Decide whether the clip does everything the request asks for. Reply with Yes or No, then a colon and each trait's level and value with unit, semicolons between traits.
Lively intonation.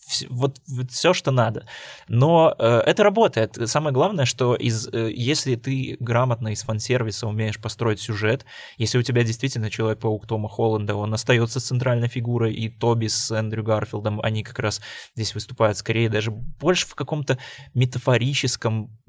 No: average, 2.9 semitones